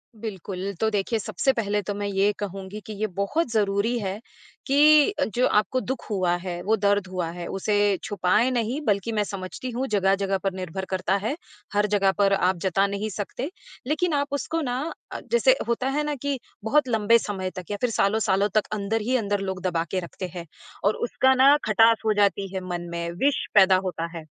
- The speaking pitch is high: Yes, high, 205 Hz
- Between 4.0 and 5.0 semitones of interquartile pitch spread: No, average, 3.6 semitones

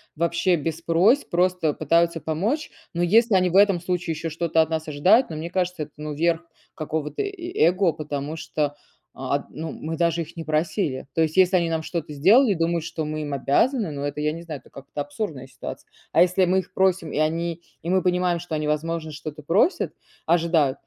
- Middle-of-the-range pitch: Yes, medium, 165 Hz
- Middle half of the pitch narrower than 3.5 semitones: Yes, average, 2.8 semitones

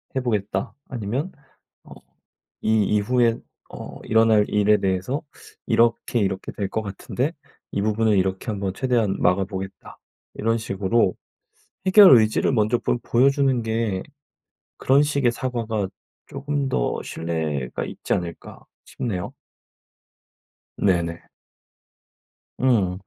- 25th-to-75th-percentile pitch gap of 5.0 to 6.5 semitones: No, average, 4.2 semitones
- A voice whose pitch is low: Yes, low, 110 Hz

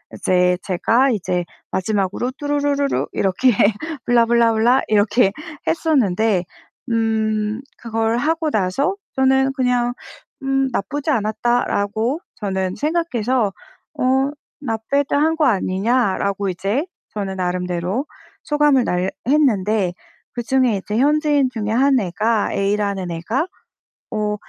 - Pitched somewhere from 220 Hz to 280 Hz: Yes, high, 225 Hz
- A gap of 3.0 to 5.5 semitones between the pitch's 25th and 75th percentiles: Yes, average, 5.1 semitones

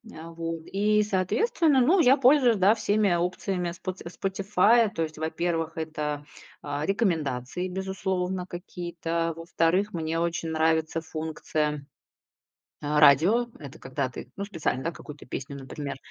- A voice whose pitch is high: No, medium, 170 Hz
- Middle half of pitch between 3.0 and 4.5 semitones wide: Yes, average, 3.8 semitones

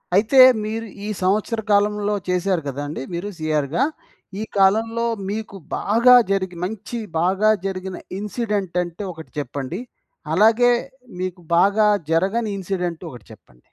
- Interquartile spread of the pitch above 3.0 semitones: Yes, average, 3.7 semitones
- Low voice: No, high, 195 Hz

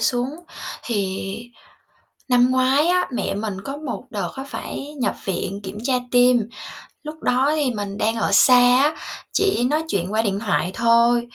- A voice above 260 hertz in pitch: No, high, 245 Hz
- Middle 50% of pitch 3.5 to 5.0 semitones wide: Yes, average, 4.5 semitones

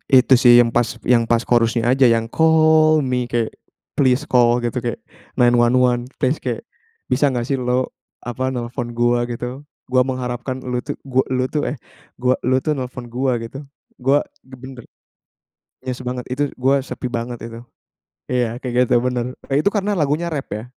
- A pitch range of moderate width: No, narrow, 1.7 semitones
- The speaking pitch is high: No, low, 125 Hz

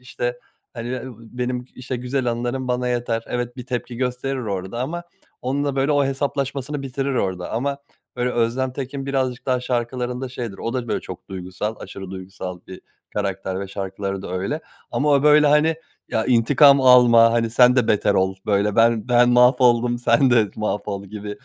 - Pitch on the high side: No, low, 120 Hz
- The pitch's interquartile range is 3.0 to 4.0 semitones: Yes, average, 3.3 semitones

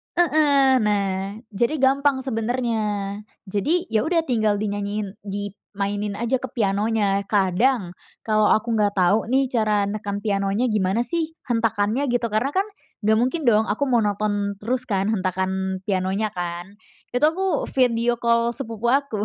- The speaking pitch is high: Yes, high, 215 Hz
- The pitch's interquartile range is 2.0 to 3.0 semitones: No, average, 3.5 semitones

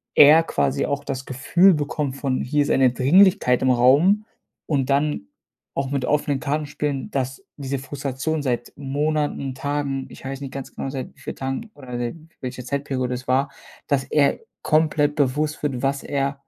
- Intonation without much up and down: Yes, narrow, 1.9 semitones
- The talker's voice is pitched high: No, medium, 140 Hz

